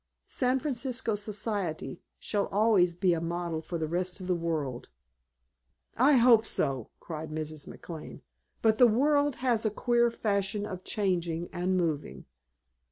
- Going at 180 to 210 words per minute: No, average, 145 wpm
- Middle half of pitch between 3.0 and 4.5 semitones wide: No, wide, 5.5 semitones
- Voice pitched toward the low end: No, high, 190 Hz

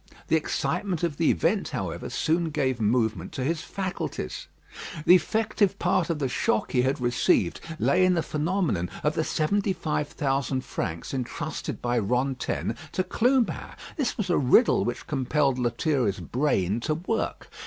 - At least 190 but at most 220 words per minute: No, average, 155 wpm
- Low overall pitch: No, medium, 150 Hz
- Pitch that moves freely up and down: Yes, wide, 6.3 semitones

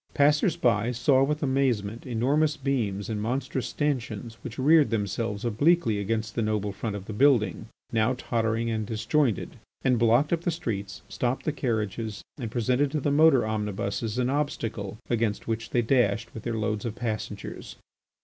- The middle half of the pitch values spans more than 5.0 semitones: No, average, 3.8 semitones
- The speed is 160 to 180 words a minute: Yes, average, 165 wpm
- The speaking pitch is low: Yes, low, 115 Hz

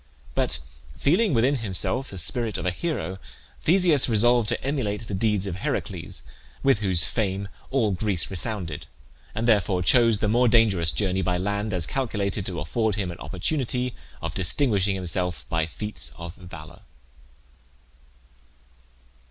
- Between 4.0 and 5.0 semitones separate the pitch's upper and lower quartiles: Yes, average, 4.6 semitones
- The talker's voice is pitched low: Yes, low, 105 Hz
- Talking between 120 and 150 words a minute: Yes, average, 145 wpm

